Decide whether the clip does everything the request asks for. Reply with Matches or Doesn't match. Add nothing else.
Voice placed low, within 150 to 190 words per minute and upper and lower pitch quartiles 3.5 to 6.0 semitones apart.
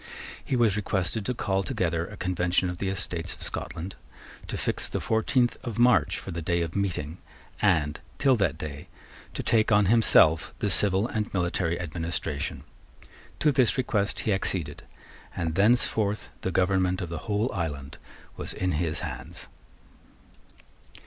Matches